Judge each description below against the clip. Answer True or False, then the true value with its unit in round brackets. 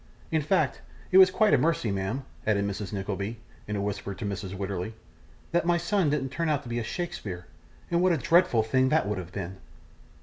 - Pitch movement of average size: False (8.8 semitones)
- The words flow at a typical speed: False (210 wpm)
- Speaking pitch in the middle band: False (115 Hz)